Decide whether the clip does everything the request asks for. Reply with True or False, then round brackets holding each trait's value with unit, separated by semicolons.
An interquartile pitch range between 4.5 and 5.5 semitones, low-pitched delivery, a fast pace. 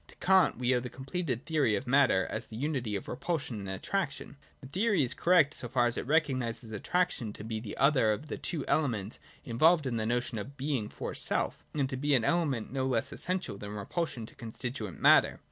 True (5.1 semitones; 130 Hz; 215 wpm)